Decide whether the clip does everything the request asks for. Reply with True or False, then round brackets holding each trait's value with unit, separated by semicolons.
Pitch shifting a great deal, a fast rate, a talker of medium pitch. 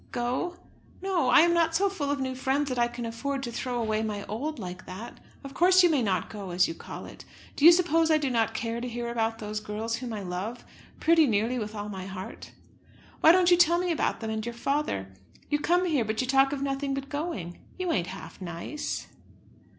False (5.8 semitones; 230 wpm; 245 Hz)